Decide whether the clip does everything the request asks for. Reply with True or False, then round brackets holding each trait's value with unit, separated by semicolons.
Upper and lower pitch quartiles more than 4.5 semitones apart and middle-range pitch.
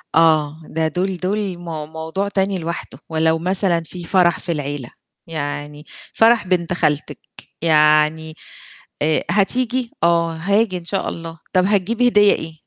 False (3.4 semitones; 170 Hz)